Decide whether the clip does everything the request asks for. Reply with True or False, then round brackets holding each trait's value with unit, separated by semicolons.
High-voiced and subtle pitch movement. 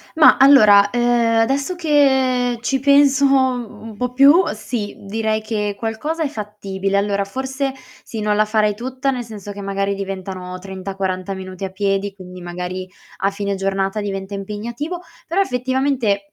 False (215 Hz; 4.9 semitones)